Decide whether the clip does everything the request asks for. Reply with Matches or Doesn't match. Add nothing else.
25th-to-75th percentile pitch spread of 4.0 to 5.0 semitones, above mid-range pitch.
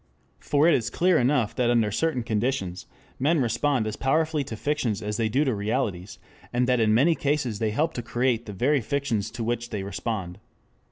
Doesn't match